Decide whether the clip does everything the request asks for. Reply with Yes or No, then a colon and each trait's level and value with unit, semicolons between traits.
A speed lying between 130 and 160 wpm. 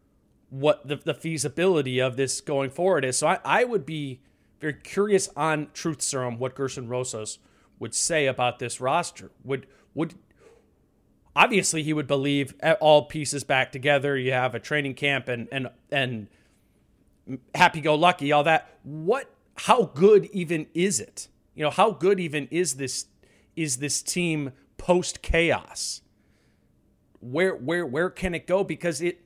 Yes: average, 155 wpm